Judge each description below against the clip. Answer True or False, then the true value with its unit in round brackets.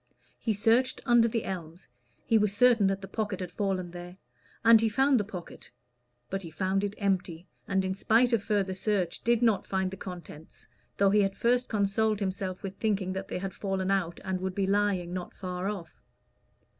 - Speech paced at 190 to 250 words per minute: True (195 wpm)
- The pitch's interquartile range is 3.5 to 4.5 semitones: False (2.5 semitones)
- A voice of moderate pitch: False (195 Hz)